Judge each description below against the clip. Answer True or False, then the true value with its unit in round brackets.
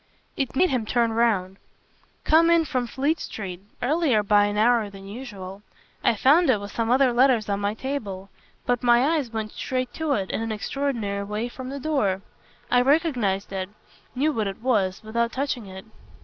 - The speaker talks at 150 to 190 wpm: True (185 wpm)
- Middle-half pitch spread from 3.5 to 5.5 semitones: True (4.7 semitones)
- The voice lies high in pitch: True (235 Hz)